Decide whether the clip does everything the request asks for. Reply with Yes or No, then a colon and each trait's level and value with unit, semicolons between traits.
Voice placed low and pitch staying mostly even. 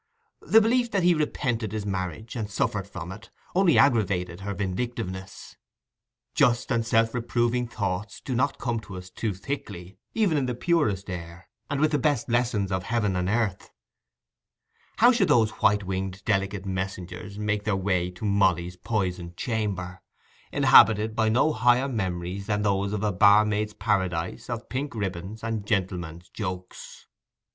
No: low, 105 Hz; average, 4.1 semitones